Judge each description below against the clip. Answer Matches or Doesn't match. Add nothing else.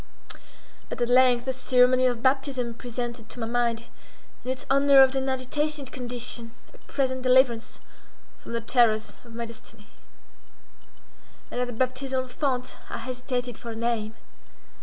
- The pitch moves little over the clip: Matches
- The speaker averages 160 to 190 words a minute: Doesn't match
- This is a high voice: Matches